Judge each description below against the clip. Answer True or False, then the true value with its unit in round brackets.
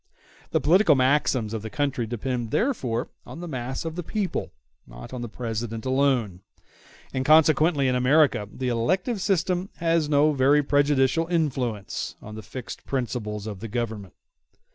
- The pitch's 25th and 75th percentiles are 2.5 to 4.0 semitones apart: False (5.2 semitones)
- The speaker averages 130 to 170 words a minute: True (155 wpm)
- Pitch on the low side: True (130 Hz)